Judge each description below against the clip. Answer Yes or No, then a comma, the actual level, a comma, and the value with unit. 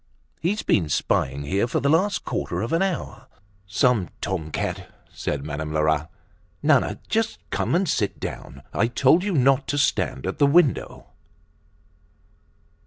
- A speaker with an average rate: Yes, average, 150 wpm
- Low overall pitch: Yes, low, 120 Hz